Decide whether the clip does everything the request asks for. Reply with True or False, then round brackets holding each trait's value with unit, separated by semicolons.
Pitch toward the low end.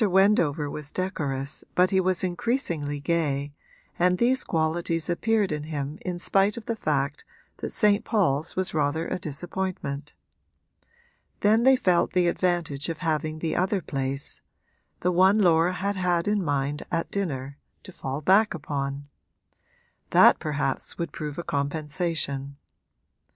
False (165 Hz)